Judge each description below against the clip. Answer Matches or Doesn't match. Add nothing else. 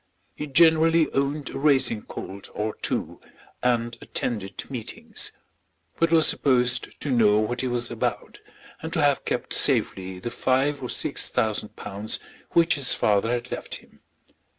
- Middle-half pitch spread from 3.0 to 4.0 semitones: Doesn't match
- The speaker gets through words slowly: Doesn't match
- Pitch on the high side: Doesn't match